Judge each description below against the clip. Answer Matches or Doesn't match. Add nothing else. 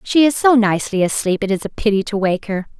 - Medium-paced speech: Doesn't match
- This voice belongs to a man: Doesn't match